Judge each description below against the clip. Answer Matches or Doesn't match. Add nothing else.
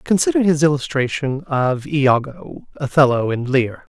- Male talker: Matches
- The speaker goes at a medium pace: Doesn't match